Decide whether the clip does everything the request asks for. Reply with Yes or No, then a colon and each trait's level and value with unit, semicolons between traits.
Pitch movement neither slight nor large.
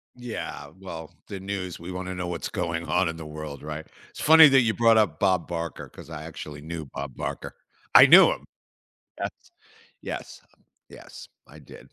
Yes: average, 3.7 semitones